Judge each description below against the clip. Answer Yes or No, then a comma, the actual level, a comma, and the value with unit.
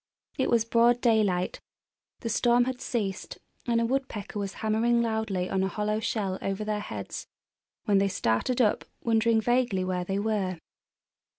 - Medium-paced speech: Yes, average, 160 wpm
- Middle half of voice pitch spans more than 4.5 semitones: No, average, 3.2 semitones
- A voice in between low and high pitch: No, high, 215 Hz